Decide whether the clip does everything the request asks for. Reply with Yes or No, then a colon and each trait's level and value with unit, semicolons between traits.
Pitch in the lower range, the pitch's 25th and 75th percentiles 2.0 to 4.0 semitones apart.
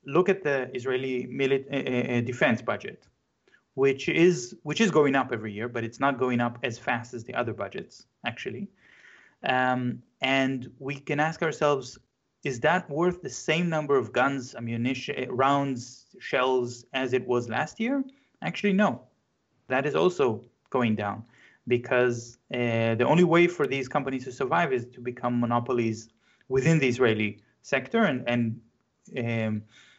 Yes: low, 130 Hz; average, 3.2 semitones